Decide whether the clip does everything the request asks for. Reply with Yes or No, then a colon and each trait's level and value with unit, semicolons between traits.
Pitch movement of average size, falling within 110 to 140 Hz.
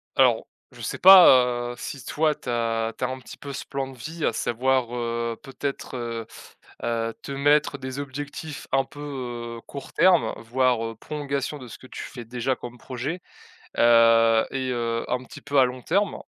Yes: average, 3.0 semitones; low, 130 Hz